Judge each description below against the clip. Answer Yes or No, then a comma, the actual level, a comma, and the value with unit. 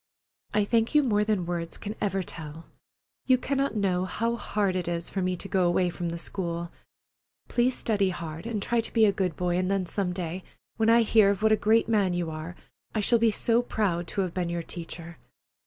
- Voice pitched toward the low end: No, high, 190 Hz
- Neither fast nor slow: No, fast, 220 wpm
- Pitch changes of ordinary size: Yes, average, 3.9 semitones